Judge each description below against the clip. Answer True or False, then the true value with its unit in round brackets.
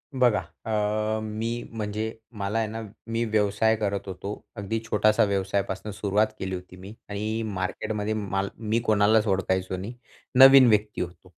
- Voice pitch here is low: True (105 Hz)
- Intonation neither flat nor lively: False (2.1 semitones)